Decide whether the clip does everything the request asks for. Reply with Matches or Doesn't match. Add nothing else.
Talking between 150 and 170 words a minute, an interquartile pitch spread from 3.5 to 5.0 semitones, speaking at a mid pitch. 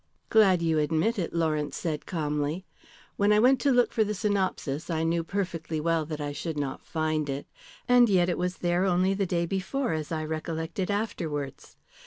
Doesn't match